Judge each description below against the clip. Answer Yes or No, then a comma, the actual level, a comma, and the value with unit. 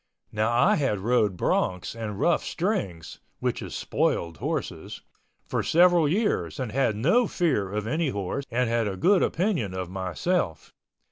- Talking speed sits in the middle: Yes, average, 155 wpm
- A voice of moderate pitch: No, low, 120 Hz